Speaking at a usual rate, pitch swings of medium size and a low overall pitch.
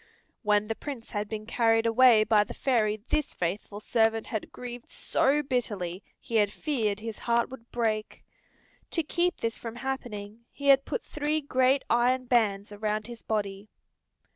No: average, 165 wpm; average, 3.3 semitones; high, 230 Hz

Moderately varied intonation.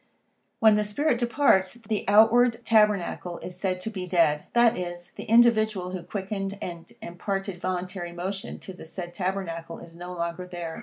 Yes: average, 3.6 semitones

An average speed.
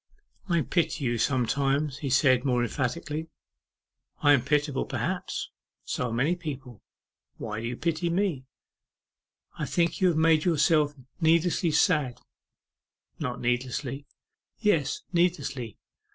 No: slow, 125 wpm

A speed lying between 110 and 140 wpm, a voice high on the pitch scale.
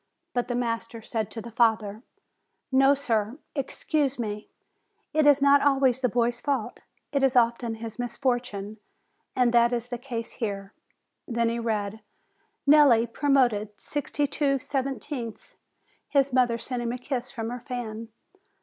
No: average, 150 wpm; high, 240 Hz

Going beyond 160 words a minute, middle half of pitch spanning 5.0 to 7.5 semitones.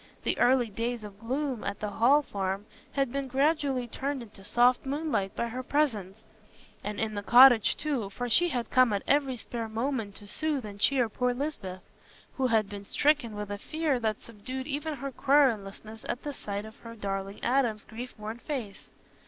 No: average, 185 wpm; average, 4.6 semitones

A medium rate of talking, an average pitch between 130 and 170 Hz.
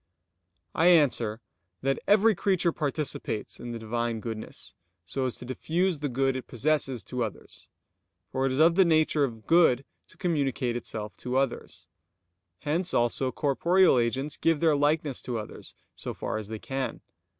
Yes: average, 160 wpm; low, 135 Hz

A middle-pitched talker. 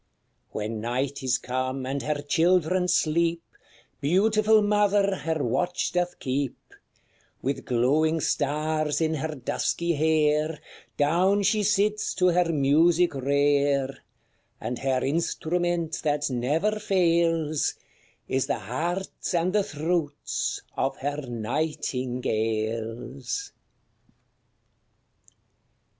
Yes: medium, 155 Hz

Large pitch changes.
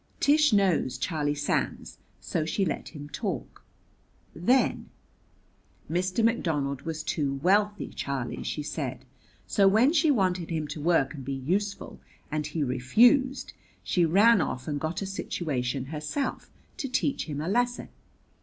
Yes: wide, 6.1 semitones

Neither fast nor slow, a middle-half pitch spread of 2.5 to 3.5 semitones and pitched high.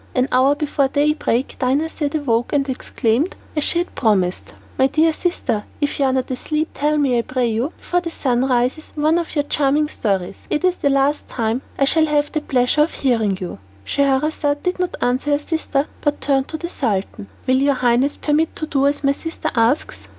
No: fast, 210 wpm; average, 3.2 semitones; very high, 280 Hz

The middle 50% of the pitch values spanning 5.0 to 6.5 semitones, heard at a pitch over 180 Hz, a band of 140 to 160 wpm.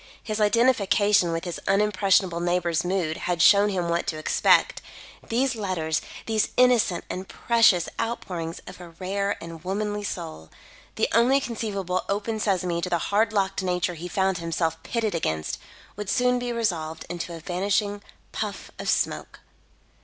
No: average, 3.6 semitones; high, 190 Hz; average, 155 wpm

